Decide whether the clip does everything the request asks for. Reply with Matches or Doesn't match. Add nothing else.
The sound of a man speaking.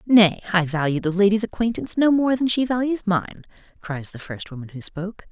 Doesn't match